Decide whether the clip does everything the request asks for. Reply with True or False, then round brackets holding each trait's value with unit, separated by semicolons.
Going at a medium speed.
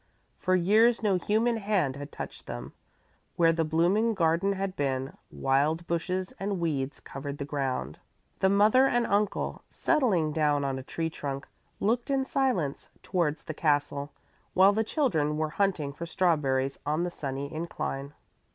True (155 wpm)